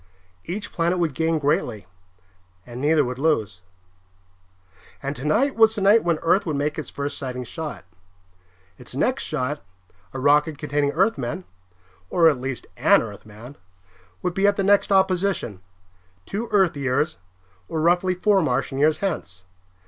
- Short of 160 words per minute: Yes, average, 150 wpm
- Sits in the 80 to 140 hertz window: No, medium, 155 Hz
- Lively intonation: Yes, wide, 5.8 semitones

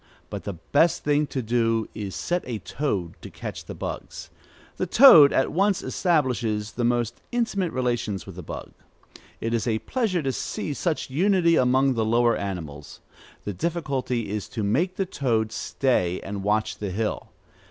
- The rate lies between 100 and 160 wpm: No, average, 170 wpm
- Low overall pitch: Yes, low, 120 Hz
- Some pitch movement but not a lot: No, wide, 6.5 semitones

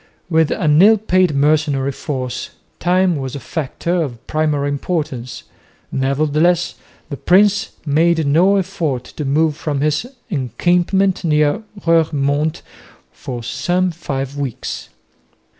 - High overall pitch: No, medium, 155 Hz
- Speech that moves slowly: Yes, slow, 115 wpm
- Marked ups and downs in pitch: No, average, 3.8 semitones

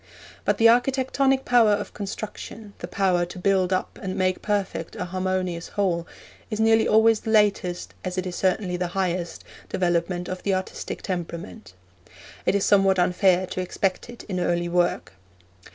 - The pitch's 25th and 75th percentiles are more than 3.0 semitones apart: No, narrow, 2.6 semitones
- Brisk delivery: No, average, 165 wpm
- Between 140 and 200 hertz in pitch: Yes, medium, 185 Hz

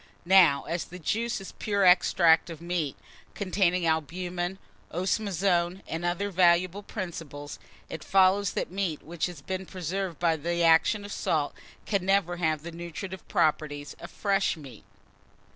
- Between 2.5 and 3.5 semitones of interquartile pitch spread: Yes, average, 2.8 semitones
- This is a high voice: No, medium, 175 Hz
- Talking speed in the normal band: Yes, average, 145 wpm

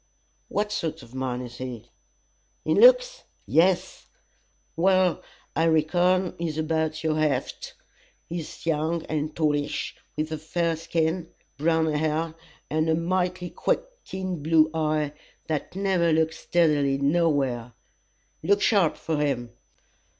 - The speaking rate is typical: No, slow, 125 wpm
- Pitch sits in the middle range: Yes, medium, 160 Hz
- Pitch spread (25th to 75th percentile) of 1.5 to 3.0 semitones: Yes, narrow, 2.4 semitones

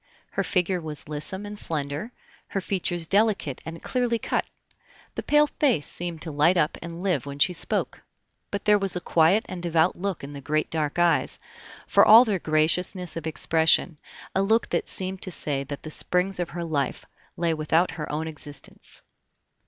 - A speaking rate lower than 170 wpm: No, average, 185 wpm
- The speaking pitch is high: No, medium, 170 Hz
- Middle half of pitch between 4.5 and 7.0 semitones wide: No, average, 3.7 semitones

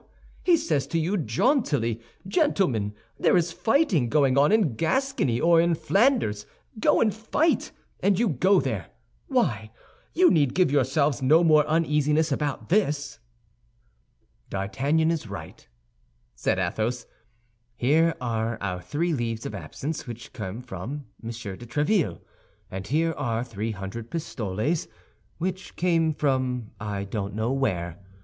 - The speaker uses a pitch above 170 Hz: No, medium, 140 Hz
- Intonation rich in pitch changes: Yes, wide, 6.8 semitones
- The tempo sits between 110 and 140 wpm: Yes, slow, 135 wpm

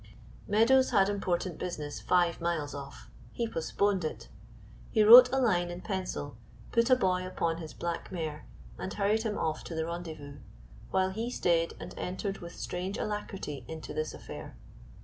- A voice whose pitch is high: No, medium, 180 Hz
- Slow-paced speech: No, average, 165 wpm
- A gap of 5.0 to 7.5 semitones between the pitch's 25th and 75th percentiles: No, average, 4.1 semitones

